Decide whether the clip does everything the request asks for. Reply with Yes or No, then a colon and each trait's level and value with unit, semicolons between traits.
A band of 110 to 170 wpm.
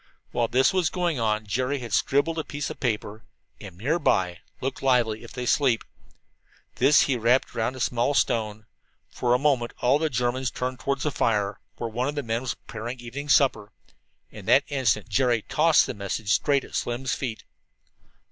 No: average, 185 wpm